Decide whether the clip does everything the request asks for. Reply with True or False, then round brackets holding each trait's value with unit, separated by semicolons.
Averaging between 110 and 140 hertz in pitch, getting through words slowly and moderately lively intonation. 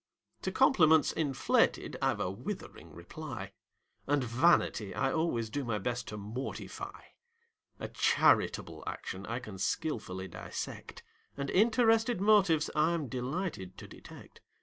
False (135 Hz; 125 wpm; 7.5 semitones)